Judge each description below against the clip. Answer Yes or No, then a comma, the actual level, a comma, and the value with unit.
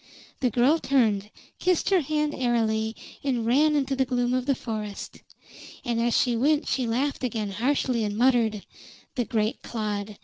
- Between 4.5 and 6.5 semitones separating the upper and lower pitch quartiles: No, average, 3.5 semitones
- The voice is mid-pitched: No, high, 240 Hz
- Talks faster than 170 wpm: No, average, 165 wpm